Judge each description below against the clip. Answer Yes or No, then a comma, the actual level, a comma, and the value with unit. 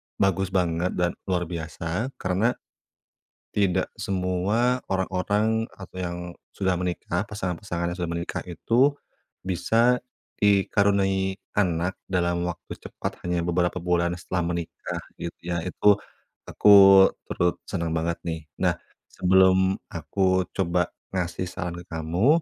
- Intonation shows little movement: Yes, narrow, 2.0 semitones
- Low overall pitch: Yes, very low, 90 Hz